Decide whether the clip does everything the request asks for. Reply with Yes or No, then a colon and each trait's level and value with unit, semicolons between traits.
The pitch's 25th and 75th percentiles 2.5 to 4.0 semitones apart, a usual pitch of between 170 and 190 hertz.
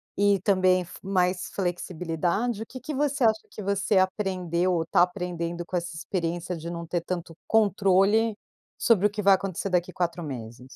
Yes: average, 2.8 semitones; medium, 185 Hz